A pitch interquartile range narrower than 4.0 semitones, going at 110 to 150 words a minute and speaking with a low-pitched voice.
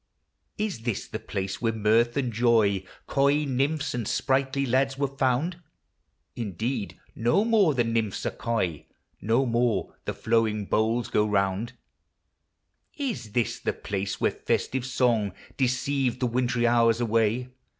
Yes: average, 3.4 semitones; average, 140 wpm; low, 120 Hz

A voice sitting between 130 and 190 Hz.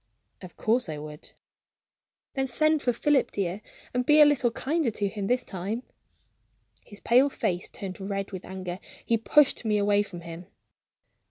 No: high, 210 Hz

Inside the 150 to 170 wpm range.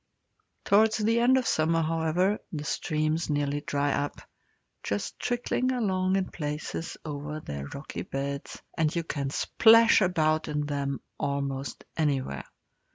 No: slow, 135 wpm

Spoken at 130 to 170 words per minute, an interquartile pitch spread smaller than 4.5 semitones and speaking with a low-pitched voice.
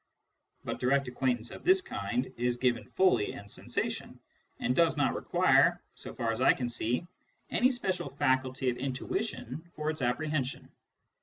Yes: average, 155 wpm; average, 4.0 semitones; low, 130 Hz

